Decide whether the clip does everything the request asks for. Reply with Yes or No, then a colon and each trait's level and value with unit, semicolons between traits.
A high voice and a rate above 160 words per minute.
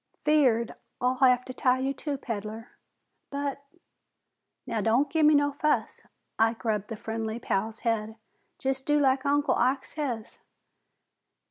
No: very high, 255 Hz; average, 140 wpm